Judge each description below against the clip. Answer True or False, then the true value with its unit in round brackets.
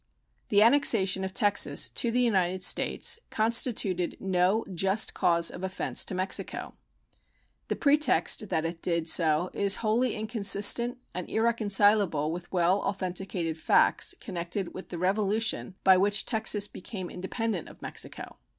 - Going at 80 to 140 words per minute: True (135 wpm)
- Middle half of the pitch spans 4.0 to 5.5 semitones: False (3.4 semitones)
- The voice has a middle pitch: False (195 Hz)